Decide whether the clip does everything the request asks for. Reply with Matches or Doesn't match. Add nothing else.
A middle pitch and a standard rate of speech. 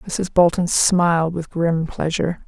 Matches